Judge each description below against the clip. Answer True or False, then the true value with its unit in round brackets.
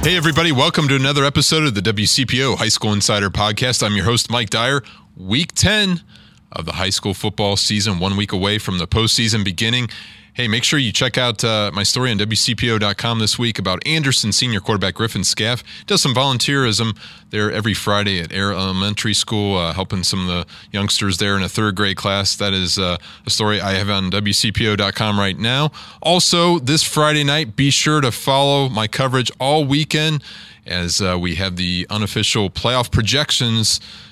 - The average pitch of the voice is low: True (110 Hz)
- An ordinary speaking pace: True (185 wpm)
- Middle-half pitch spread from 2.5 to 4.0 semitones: False (4.6 semitones)